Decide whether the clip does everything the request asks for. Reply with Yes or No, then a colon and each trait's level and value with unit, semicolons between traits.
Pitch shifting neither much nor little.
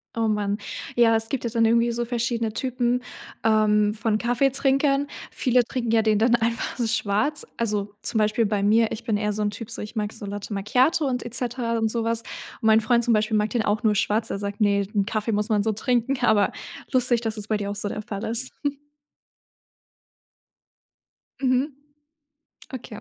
No: narrow, 2.3 semitones